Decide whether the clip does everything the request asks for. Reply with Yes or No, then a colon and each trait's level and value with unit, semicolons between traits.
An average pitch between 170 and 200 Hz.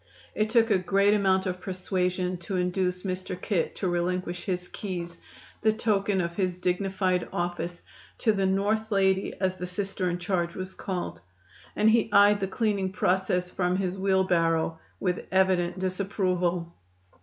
Yes: medium, 185 Hz